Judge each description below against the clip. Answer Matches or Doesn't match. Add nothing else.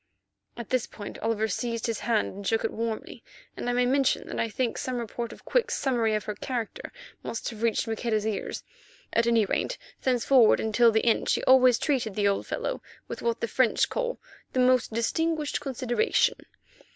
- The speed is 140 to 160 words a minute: Doesn't match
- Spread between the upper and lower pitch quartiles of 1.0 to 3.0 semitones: Matches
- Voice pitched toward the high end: Matches